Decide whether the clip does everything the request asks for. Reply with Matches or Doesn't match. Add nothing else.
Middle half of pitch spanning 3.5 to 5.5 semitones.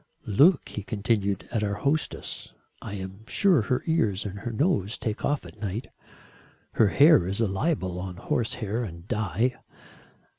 Matches